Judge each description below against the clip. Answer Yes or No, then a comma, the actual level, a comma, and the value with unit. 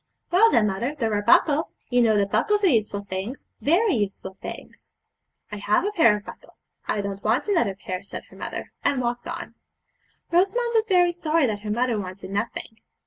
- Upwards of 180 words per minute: Yes, average, 195 wpm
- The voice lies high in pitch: Yes, high, 235 Hz